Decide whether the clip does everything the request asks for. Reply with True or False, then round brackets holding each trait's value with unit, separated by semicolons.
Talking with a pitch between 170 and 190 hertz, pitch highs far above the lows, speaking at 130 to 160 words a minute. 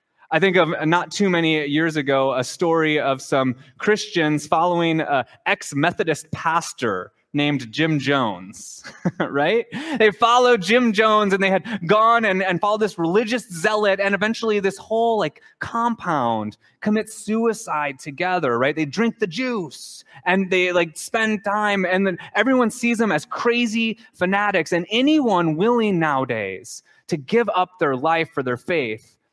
True (185 Hz; 6.0 semitones; 150 wpm)